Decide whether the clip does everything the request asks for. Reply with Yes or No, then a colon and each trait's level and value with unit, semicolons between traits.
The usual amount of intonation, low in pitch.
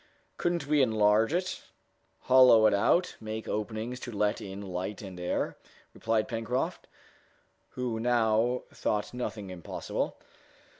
Yes: average, 3.1 semitones; low, 110 Hz